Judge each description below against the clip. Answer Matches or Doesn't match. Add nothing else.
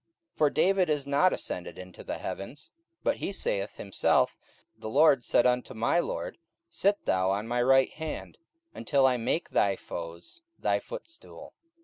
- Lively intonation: Matches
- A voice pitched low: Matches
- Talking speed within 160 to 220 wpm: Matches